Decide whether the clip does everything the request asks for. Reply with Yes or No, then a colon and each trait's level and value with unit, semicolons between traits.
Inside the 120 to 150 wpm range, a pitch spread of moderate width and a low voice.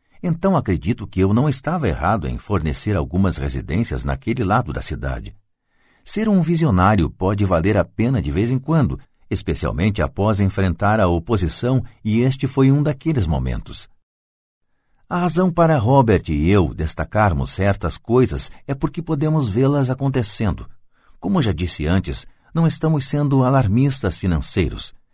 No: average, 145 wpm; wide, 7.7 semitones; low, 105 Hz